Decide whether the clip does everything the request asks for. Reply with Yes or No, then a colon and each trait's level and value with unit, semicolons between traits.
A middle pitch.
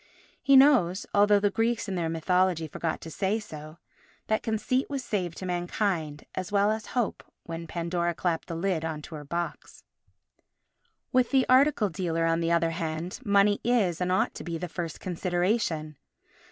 Yes: medium, 180 Hz